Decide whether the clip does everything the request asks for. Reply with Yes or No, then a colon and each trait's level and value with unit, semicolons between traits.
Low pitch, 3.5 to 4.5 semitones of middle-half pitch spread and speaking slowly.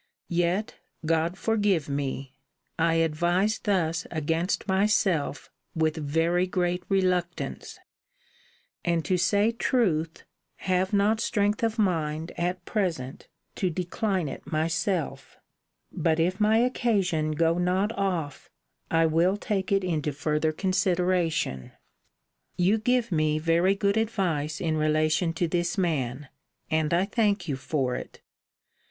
No: medium, 175 Hz; average, 3.8 semitones; slow, 120 wpm